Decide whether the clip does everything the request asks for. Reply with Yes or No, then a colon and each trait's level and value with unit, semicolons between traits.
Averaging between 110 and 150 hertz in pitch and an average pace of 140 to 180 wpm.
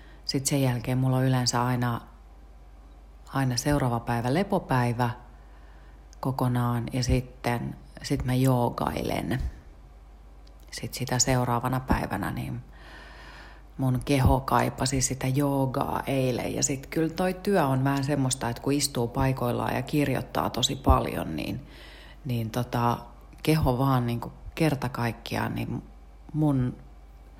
No: low, 125 Hz; average, 120 wpm